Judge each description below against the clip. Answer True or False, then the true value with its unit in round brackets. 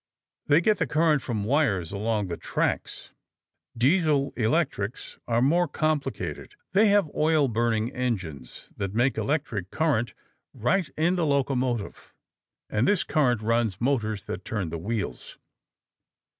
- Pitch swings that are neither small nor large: False (6.3 semitones)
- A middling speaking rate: False (130 wpm)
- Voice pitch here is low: True (125 Hz)